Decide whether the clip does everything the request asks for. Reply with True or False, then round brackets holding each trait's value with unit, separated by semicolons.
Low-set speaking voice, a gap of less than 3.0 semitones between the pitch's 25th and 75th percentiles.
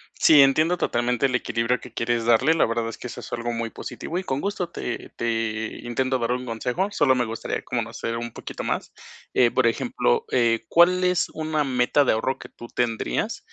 False (125 Hz; 4.1 semitones)